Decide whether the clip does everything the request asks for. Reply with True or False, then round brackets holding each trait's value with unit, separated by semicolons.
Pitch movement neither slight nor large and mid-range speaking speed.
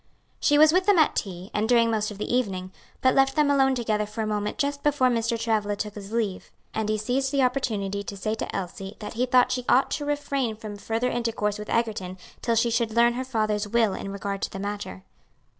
False (3.4 semitones; 230 wpm)